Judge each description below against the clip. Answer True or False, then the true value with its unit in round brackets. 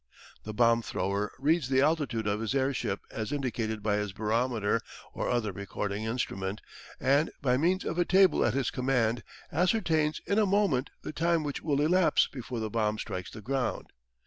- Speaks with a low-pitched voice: True (125 Hz)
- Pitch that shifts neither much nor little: False (5.7 semitones)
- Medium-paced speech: True (175 wpm)